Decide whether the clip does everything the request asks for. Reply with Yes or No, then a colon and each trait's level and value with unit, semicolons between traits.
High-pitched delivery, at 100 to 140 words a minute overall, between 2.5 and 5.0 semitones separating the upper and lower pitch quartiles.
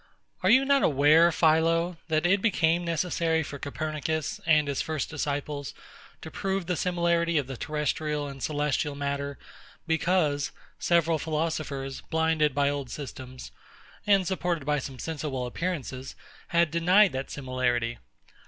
No: medium, 155 Hz; slow, 135 wpm; average, 3.0 semitones